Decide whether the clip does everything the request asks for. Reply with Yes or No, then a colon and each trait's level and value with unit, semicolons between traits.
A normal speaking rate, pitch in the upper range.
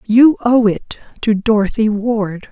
Yes: average, 145 wpm; high, 220 Hz